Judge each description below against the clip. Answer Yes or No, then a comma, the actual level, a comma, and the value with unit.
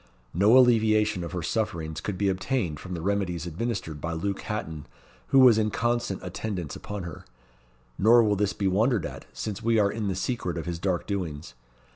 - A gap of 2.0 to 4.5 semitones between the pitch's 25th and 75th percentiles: Yes, average, 4.0 semitones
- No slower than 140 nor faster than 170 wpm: No, average, 190 wpm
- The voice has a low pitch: Yes, low, 100 Hz